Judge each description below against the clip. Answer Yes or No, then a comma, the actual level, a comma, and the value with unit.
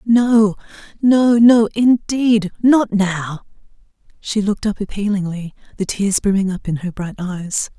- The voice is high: Yes, high, 205 Hz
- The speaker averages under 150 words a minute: Yes, average, 140 wpm